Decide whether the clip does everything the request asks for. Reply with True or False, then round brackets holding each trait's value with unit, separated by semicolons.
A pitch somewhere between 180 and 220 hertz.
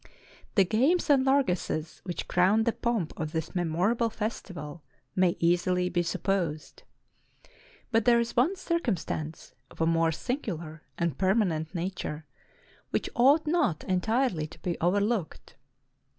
True (185 Hz)